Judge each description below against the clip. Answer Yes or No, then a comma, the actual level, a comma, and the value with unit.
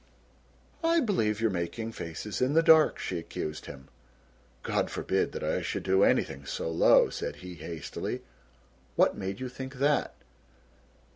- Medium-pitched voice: No, low, 105 Hz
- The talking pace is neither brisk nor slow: Yes, average, 150 wpm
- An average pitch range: No, wide, 8.2 semitones